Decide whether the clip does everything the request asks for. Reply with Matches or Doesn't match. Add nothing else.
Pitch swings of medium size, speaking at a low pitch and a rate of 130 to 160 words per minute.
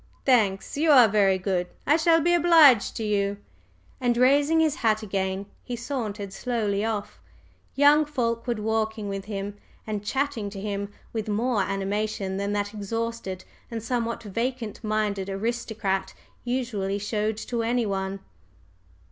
Doesn't match